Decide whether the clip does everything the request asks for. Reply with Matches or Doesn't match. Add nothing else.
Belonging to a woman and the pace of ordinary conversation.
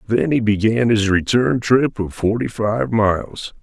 Doesn't match